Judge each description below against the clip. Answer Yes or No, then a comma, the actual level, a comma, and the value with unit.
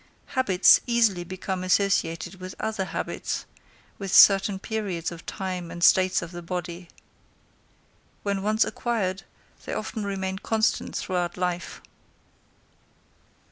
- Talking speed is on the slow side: Yes, slow, 115 wpm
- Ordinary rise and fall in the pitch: No, narrow, 2.2 semitones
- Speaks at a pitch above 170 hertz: Yes, high, 190 Hz